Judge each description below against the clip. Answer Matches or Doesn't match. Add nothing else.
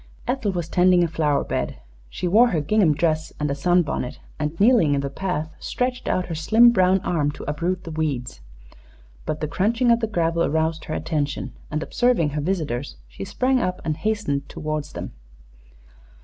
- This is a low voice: Doesn't match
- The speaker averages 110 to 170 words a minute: Doesn't match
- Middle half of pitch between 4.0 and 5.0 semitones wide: Matches